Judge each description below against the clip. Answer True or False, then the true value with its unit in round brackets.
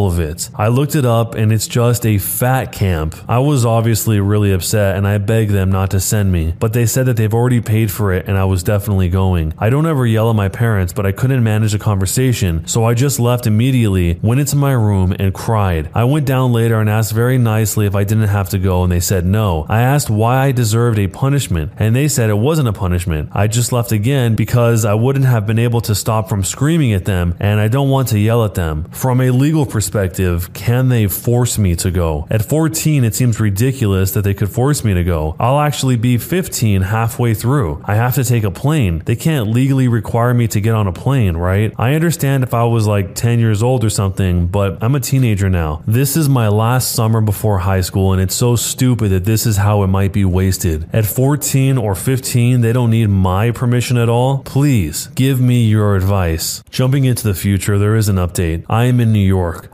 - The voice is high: False (110 Hz)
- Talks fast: True (230 wpm)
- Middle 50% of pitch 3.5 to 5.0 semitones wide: True (4.0 semitones)